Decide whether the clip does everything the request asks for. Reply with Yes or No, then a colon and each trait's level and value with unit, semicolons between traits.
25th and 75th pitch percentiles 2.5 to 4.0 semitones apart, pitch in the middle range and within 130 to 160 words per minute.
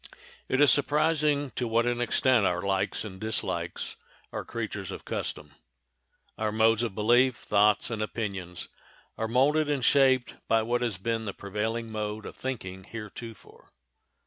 No: average, 3.3 semitones; low, 115 Hz; average, 150 wpm